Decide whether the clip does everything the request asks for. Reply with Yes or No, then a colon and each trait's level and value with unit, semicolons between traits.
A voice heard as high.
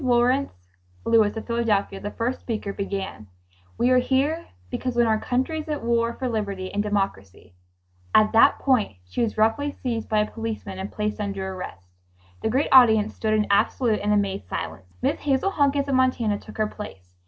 Yes: high, 220 Hz